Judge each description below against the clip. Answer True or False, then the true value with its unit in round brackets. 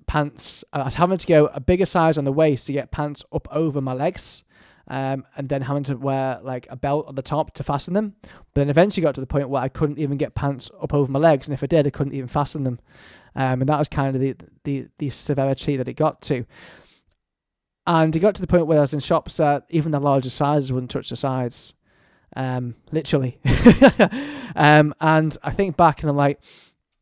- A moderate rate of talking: False (230 wpm)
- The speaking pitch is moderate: True (145 Hz)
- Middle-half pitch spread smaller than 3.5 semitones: True (2.7 semitones)